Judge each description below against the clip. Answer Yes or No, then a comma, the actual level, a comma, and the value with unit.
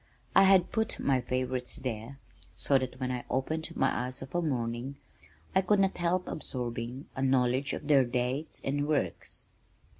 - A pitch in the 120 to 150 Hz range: Yes, low, 135 Hz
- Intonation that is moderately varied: Yes, average, 3.7 semitones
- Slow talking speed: No, average, 170 wpm